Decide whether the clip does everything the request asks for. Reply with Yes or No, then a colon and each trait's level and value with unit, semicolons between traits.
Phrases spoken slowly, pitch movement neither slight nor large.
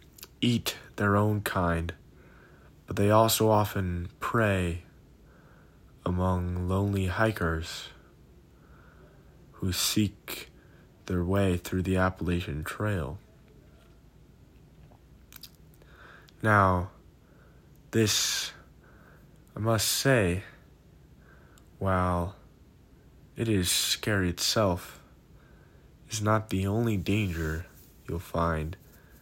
Yes: slow, 75 wpm; average, 3.4 semitones